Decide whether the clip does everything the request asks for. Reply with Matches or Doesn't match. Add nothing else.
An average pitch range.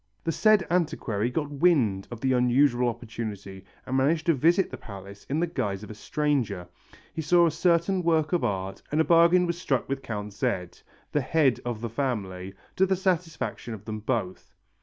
Doesn't match